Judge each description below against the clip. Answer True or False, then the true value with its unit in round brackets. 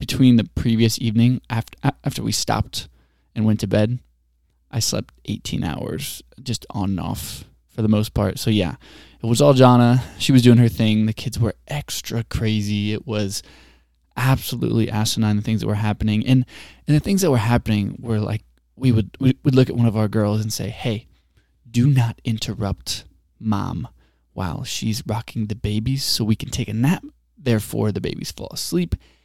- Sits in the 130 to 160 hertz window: False (110 Hz)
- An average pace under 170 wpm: False (185 wpm)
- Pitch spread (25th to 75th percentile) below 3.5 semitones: True (2.9 semitones)